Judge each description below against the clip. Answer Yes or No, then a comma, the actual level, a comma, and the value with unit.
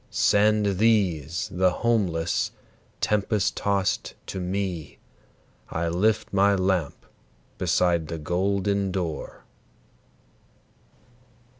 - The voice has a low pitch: Yes, very low, 95 Hz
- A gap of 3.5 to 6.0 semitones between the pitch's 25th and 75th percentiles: No, narrow, 2.6 semitones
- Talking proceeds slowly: Yes, slow, 85 wpm